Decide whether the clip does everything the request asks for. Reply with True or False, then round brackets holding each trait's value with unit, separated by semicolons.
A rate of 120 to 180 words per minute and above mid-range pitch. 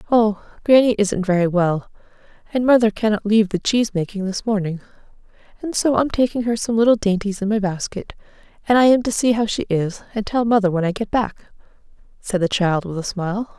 False (205 wpm; 210 Hz)